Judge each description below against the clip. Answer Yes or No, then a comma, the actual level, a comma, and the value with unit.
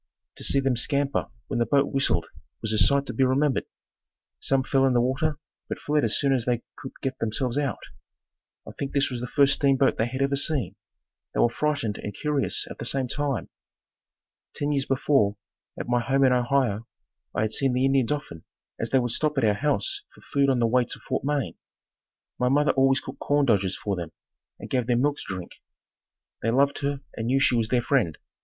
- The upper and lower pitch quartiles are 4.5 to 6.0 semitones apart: No, average, 3.0 semitones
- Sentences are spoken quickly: Yes, fast, 215 wpm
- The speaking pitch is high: No, low, 130 Hz